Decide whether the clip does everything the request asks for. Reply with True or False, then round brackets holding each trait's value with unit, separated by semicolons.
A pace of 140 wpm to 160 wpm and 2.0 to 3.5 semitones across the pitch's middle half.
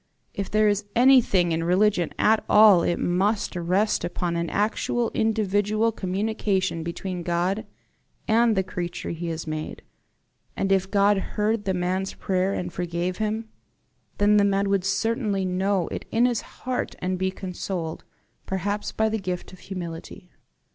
True (155 wpm; 2.9 semitones)